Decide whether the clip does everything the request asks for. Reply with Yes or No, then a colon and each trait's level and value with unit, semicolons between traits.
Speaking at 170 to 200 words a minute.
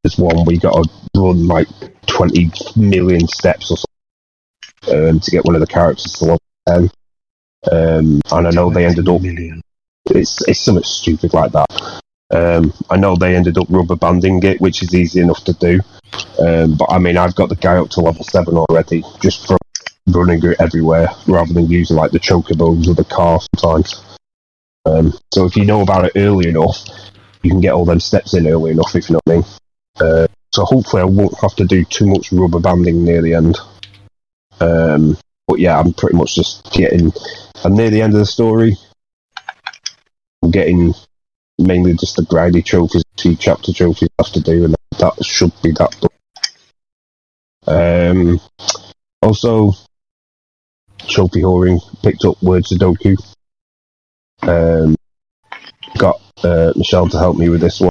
Yes: average, 180 wpm